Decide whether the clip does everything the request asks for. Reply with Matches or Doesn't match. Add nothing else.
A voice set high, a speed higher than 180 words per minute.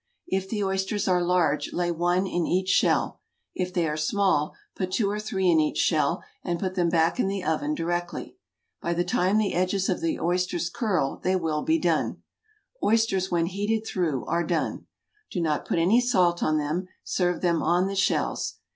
Doesn't match